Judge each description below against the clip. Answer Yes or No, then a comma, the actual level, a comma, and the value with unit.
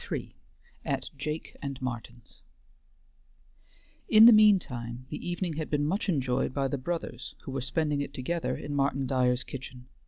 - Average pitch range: Yes, average, 4.1 semitones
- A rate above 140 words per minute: Yes, average, 160 wpm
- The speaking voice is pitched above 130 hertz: Yes, medium, 140 Hz